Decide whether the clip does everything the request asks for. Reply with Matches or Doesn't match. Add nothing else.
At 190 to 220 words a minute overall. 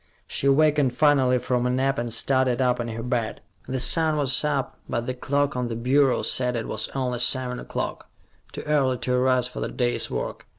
Matches